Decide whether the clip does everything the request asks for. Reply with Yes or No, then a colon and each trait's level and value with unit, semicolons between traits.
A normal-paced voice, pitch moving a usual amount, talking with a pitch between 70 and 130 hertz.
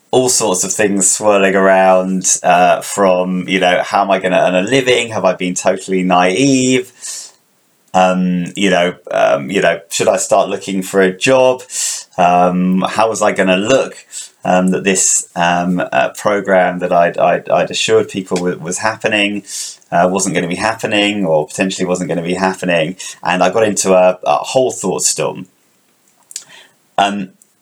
No: average, 175 wpm; narrow, 2.0 semitones; very low, 95 Hz